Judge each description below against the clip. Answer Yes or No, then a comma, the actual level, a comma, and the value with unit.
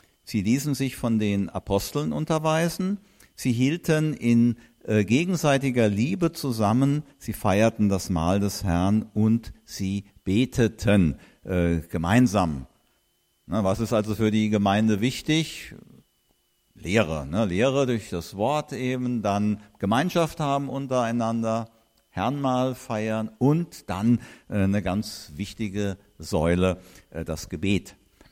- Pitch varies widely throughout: No, average, 4.5 semitones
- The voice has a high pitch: No, low, 110 Hz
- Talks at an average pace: No, slow, 120 wpm